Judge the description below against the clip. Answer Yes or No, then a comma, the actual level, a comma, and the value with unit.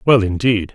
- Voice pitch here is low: Yes, low, 105 Hz